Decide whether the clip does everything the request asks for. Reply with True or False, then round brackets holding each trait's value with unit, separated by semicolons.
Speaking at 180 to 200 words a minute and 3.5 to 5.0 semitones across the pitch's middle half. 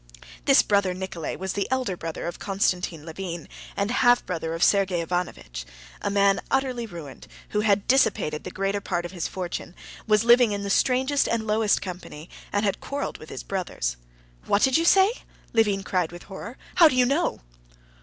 True (185 wpm; 4.7 semitones)